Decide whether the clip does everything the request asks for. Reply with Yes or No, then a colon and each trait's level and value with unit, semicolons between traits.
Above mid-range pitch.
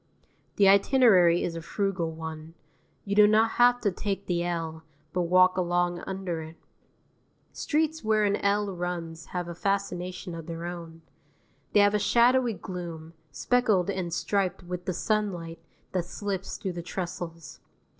No: medium, 180 Hz